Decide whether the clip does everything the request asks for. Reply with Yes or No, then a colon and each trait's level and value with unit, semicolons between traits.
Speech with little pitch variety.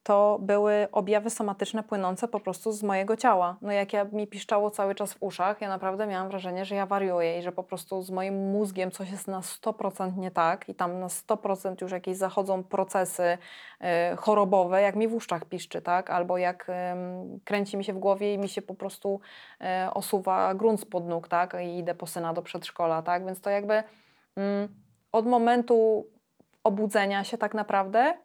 Yes: narrow, 2.3 semitones